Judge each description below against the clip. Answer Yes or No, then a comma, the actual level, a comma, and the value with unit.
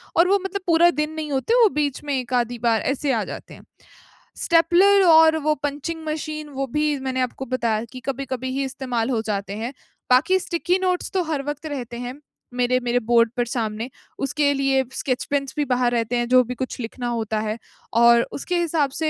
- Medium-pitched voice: No, very high, 265 Hz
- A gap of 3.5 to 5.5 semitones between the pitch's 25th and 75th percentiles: Yes, average, 4.2 semitones